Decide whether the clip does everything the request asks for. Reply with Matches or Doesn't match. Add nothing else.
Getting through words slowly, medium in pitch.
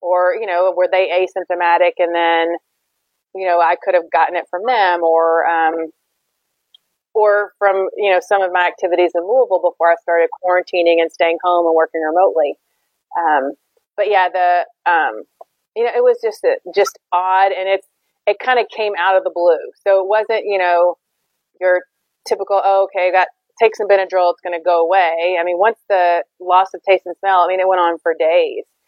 Doesn't match